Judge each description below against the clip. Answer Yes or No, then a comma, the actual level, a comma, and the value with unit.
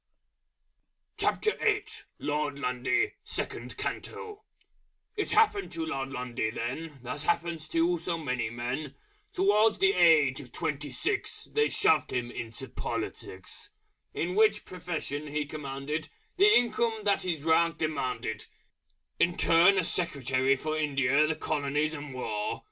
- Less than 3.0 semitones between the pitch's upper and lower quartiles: No, average, 4.8 semitones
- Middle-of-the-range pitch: Yes, medium, 155 Hz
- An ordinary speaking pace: No, slow, 125 wpm